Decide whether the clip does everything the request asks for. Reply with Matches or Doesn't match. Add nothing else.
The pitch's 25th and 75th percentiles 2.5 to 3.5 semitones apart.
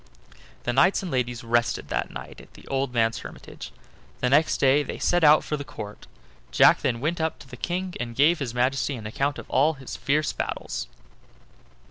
Doesn't match